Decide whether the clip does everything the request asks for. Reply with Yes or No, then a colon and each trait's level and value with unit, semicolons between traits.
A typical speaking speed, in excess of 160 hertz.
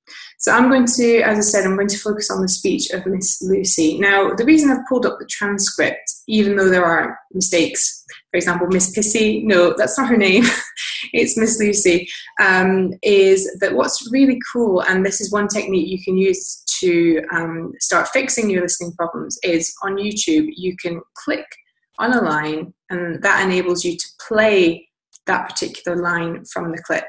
Yes: average, 185 wpm; high, 190 Hz